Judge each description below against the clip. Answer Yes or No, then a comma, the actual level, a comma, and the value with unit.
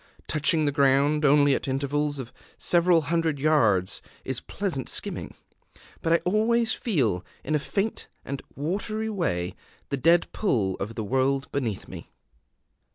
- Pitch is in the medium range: Yes, medium, 145 Hz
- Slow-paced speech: No, average, 145 wpm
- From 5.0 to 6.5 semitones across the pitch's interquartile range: No, average, 4.2 semitones